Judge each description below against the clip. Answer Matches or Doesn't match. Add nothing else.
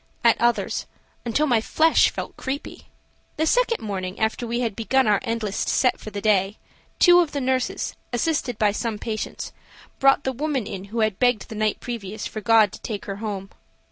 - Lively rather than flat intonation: Doesn't match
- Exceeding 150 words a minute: Matches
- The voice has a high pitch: Matches